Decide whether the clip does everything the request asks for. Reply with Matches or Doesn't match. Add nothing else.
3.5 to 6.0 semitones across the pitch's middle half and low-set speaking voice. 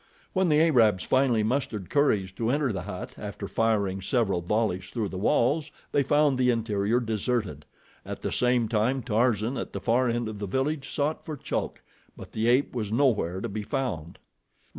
Matches